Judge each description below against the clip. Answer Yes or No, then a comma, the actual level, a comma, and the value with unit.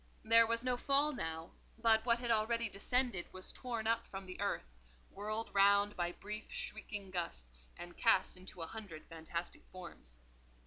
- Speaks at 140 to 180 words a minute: Yes, average, 165 wpm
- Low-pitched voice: No, high, 205 Hz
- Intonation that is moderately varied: Yes, average, 4.6 semitones